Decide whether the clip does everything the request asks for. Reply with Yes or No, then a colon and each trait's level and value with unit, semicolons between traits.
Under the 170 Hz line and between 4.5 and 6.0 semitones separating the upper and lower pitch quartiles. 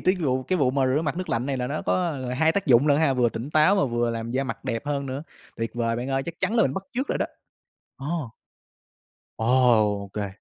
Yes: low, 135 Hz; average, 5.0 semitones